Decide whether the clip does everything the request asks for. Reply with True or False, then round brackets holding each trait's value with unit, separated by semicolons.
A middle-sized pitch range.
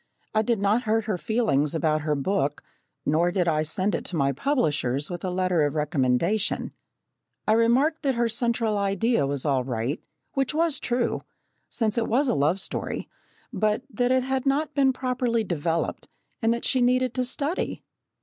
False (8.1 semitones)